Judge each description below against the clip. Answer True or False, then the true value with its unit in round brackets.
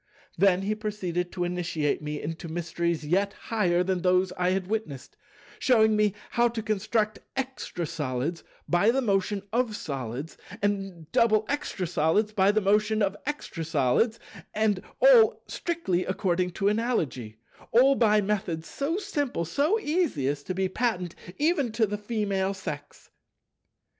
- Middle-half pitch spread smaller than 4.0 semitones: False (4.4 semitones)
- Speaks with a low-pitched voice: False (195 Hz)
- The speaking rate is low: False (150 wpm)